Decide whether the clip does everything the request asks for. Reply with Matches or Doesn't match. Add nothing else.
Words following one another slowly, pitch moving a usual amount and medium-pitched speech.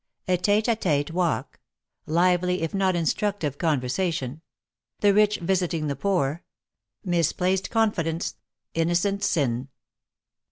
Matches